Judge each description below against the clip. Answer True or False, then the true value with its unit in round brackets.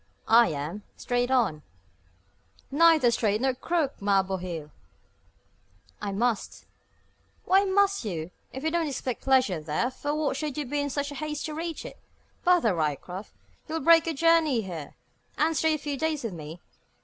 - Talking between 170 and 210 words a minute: False (160 wpm)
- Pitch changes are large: True (8.1 semitones)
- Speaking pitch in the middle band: False (265 Hz)